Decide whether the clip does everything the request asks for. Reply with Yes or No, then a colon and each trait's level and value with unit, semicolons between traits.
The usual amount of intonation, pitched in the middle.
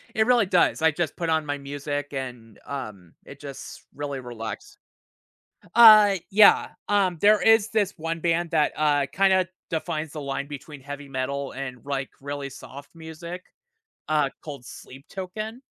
Yes: average, 4.6 semitones; medium, 150 Hz